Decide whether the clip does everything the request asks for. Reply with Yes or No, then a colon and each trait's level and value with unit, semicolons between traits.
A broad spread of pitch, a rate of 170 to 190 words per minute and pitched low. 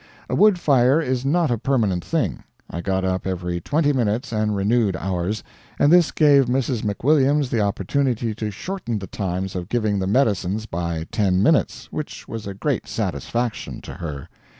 Yes: wide, 6.0 semitones; average, 175 wpm; low, 110 Hz